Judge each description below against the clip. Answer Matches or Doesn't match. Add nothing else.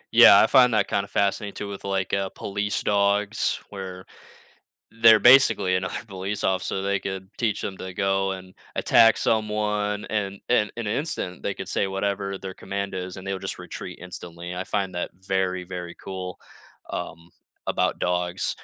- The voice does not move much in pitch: Matches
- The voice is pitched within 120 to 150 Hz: Doesn't match